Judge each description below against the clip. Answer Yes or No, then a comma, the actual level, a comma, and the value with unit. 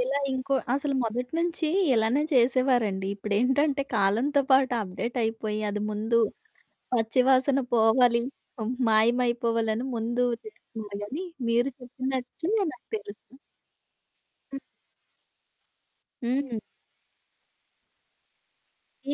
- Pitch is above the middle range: Yes, high, 245 Hz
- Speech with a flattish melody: No, average, 3.2 semitones